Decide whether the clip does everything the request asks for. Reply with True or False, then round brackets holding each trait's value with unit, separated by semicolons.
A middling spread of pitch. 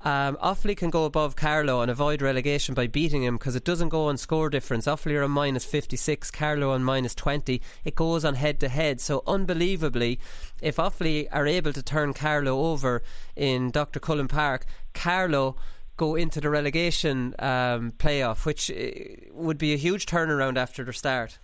True (3.1 semitones)